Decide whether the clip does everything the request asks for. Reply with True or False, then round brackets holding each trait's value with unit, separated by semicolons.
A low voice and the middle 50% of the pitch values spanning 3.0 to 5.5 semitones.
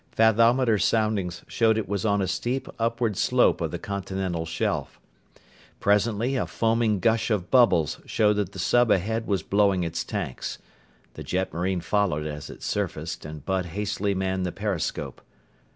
True (100 Hz; 3.4 semitones)